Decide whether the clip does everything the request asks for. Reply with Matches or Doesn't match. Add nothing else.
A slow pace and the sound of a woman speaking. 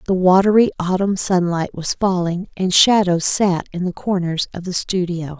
Doesn't match